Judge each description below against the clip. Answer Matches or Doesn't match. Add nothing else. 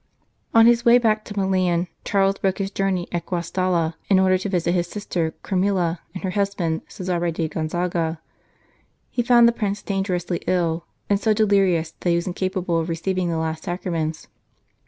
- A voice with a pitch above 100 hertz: Matches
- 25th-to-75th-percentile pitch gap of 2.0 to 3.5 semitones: Matches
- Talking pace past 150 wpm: Matches